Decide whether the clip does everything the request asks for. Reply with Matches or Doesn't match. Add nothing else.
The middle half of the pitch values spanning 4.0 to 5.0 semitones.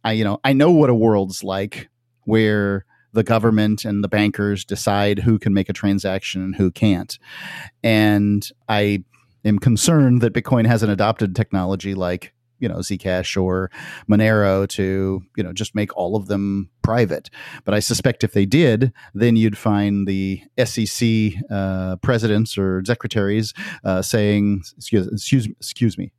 Doesn't match